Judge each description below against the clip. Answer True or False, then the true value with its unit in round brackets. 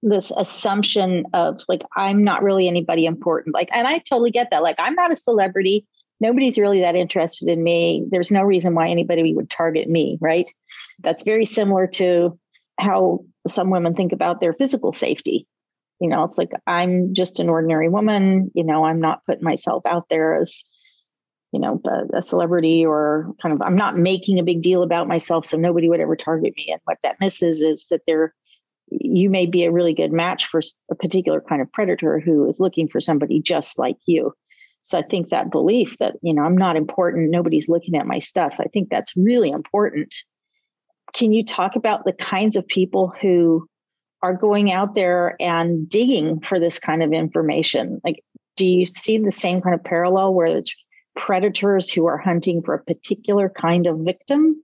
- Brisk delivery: False (195 wpm)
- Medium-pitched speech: True (180 Hz)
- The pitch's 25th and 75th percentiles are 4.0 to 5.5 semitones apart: False (3.2 semitones)